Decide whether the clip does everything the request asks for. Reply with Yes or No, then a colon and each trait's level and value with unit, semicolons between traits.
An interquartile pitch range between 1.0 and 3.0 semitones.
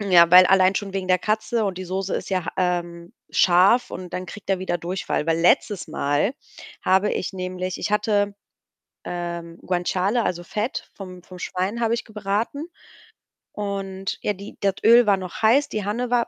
Yes: narrow, 2.6 semitones